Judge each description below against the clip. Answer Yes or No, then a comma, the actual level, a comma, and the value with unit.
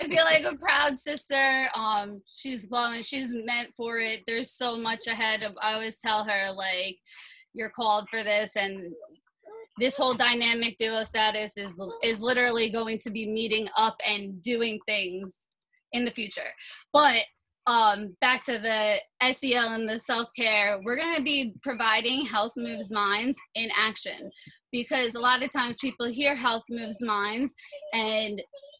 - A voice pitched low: No, high, 230 Hz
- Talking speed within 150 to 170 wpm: Yes, average, 160 wpm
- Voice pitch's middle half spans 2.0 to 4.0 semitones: Yes, average, 2.9 semitones